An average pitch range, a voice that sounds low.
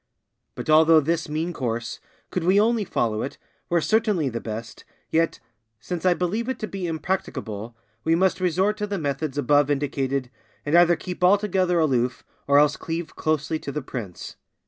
No: average, 4.8 semitones; medium, 160 Hz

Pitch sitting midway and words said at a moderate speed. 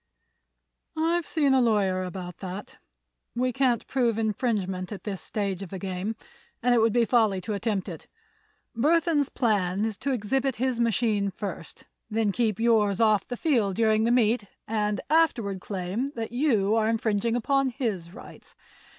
No: high, 220 Hz; average, 160 wpm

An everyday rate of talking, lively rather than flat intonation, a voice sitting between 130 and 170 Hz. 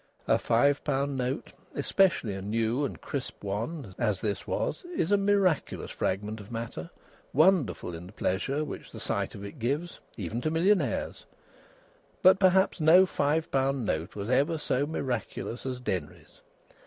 Yes: average, 155 wpm; wide, 7.1 semitones; low, 135 Hz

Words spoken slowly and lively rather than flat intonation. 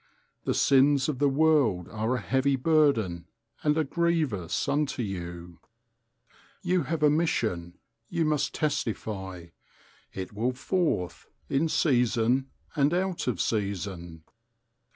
Yes: slow, 120 wpm; wide, 7.8 semitones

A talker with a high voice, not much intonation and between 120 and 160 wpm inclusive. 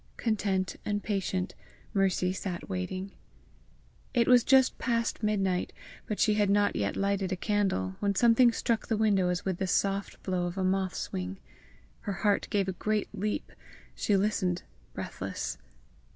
Yes: high, 195 Hz; narrow, 2.3 semitones; average, 155 wpm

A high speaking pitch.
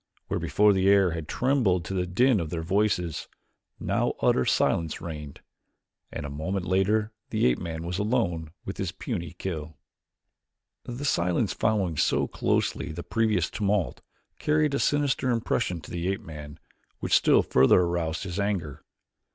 No: very low, 90 Hz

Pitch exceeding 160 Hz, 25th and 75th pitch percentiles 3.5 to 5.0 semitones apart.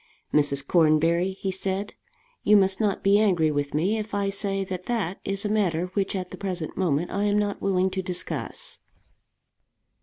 No: high, 190 Hz; narrow, 2.6 semitones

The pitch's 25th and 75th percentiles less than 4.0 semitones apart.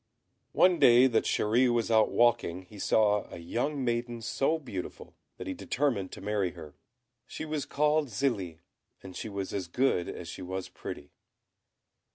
No: wide, 5.6 semitones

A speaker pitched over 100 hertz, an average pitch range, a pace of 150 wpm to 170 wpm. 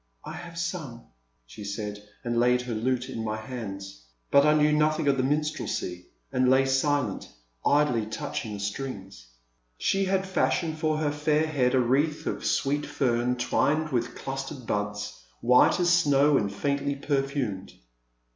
Yes: low, 135 Hz; average, 4.6 semitones; average, 155 wpm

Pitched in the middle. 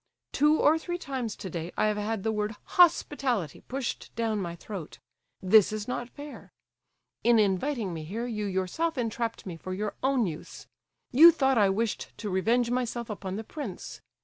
No: high, 225 Hz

